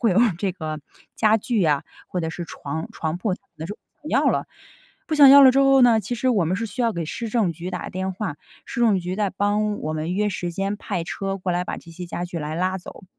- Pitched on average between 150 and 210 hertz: Yes, high, 190 Hz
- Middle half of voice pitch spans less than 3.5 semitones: No, average, 4.1 semitones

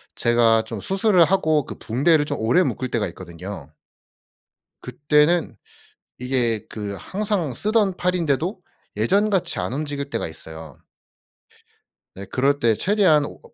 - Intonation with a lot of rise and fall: Yes, wide, 8.1 semitones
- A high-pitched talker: No, medium, 140 Hz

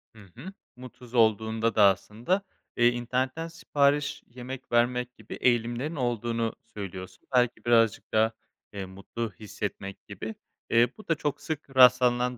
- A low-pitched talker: Yes, low, 120 Hz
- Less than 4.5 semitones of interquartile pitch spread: Yes, narrow, 2.6 semitones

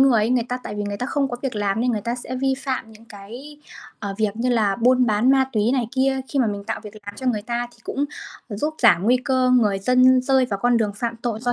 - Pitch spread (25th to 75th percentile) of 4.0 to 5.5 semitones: No, average, 3.3 semitones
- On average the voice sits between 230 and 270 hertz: Yes, high, 240 Hz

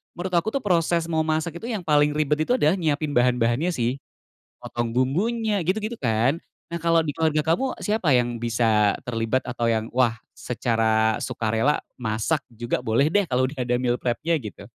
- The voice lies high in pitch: No, medium, 140 Hz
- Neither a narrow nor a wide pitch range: No, wide, 5.9 semitones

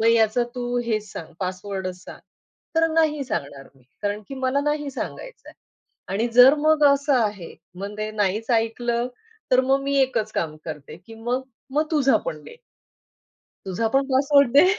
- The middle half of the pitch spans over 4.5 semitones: Yes, average, 5.1 semitones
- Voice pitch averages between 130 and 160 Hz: No, high, 240 Hz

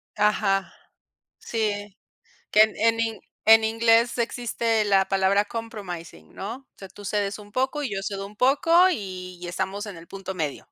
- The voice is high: Yes, high, 205 Hz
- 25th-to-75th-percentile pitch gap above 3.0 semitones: No, average, 2.7 semitones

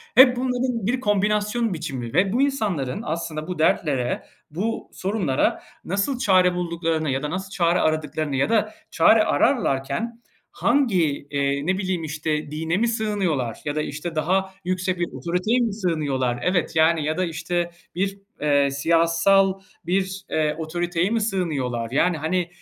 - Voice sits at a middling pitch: Yes, medium, 175 Hz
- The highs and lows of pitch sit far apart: No, average, 4.4 semitones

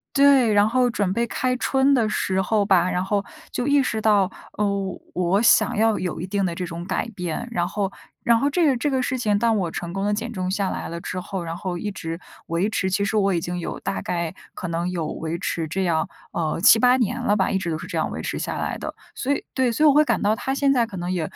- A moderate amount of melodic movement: Yes, average, 4.8 semitones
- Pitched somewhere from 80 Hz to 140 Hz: No, high, 200 Hz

